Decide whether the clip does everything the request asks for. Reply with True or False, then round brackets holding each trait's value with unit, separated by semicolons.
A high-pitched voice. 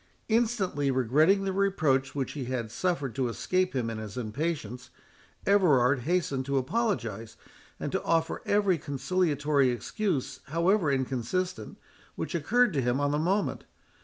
False (145 Hz)